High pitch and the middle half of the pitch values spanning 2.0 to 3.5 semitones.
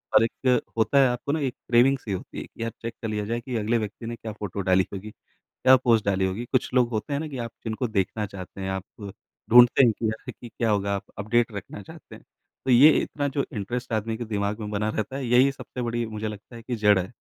No: low, 115 Hz; average, 3.0 semitones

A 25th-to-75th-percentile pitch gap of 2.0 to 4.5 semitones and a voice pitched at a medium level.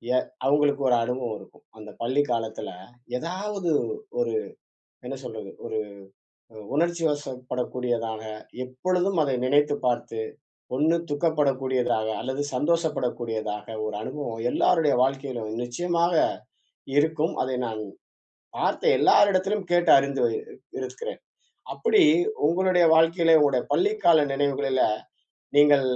No: average, 5.2 semitones; medium, 145 Hz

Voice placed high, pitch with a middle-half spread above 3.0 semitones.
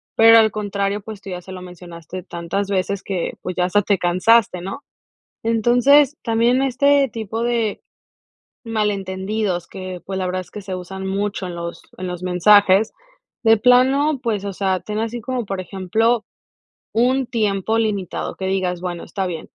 Yes: high, 200 Hz; average, 3.5 semitones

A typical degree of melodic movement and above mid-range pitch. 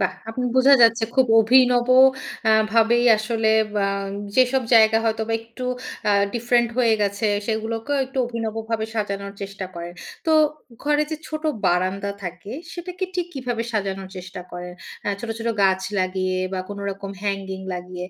Yes: average, 3.6 semitones; high, 220 Hz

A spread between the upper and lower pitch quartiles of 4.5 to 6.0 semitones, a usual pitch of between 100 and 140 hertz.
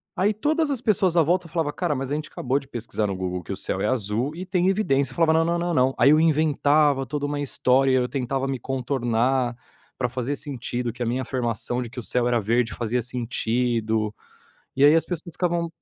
Yes: average, 4.8 semitones; low, 135 Hz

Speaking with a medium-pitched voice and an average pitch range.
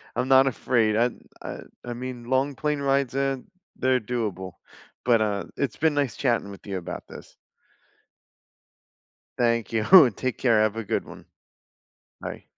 No: low, 120 Hz; average, 3.5 semitones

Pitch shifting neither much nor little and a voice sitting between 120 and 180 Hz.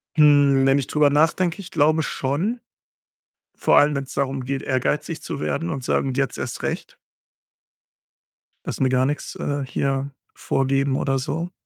No: narrow, 2.0 semitones; medium, 140 Hz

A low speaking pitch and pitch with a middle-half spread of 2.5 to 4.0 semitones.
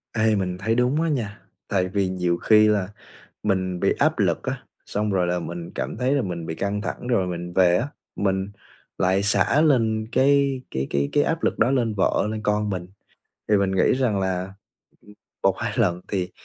Yes: low, 100 Hz; average, 3.7 semitones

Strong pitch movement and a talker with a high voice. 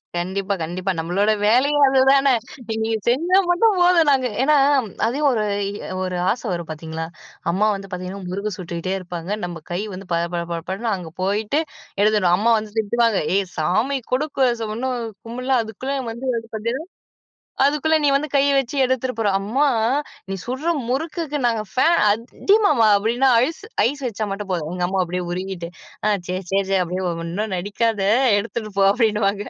Yes: wide, 5.7 semitones; high, 215 Hz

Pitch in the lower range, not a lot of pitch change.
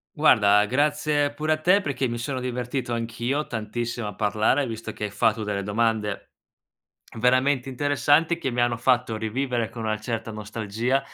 No: low, 120 Hz; average, 3.7 semitones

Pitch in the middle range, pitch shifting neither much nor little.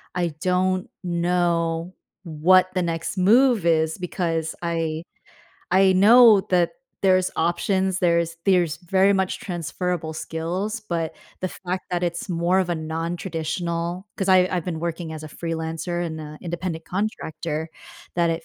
No: medium, 175 Hz; narrow, 2.1 semitones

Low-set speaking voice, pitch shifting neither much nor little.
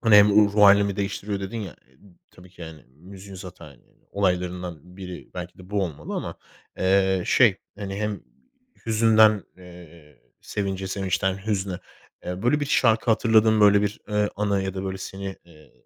No: very low, 95 Hz; narrow, 2.3 semitones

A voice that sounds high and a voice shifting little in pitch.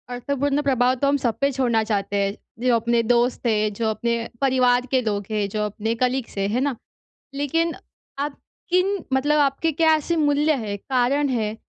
No: very high, 250 Hz; average, 4.3 semitones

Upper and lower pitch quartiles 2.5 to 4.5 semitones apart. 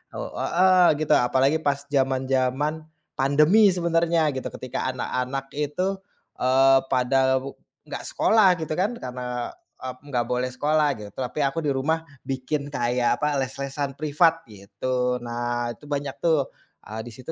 Yes: average, 3.5 semitones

